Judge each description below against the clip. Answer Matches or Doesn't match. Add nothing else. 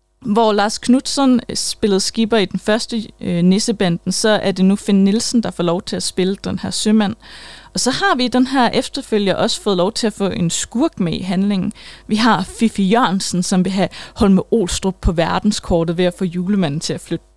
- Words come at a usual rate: Matches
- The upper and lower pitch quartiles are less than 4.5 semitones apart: Matches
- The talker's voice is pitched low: Doesn't match